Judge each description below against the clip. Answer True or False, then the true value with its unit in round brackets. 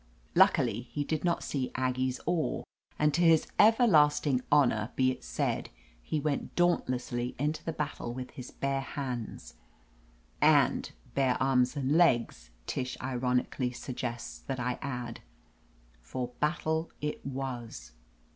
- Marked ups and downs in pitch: False (3.2 semitones)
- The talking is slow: True (130 wpm)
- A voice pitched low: True (130 Hz)